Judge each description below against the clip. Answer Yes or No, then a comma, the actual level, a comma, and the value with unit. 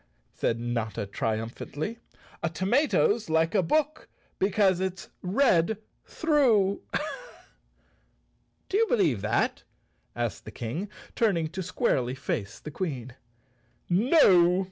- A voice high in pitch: No, medium, 180 Hz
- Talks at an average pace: No, slow, 105 wpm